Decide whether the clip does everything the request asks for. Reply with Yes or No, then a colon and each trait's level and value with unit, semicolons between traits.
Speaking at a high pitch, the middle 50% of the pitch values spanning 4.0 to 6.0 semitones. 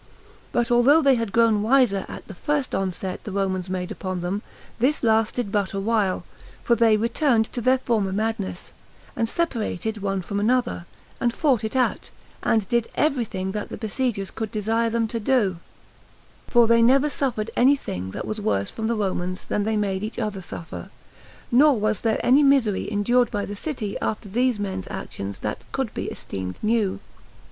No: high, 220 Hz; average, 3.5 semitones